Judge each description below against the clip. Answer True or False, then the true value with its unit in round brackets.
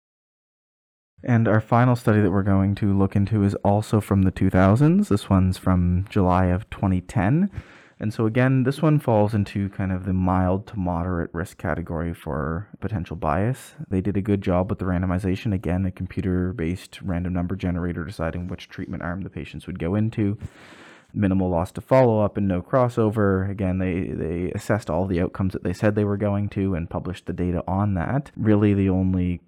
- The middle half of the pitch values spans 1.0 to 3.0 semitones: True (2.5 semitones)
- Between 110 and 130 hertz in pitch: False (95 Hz)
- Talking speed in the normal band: True (190 wpm)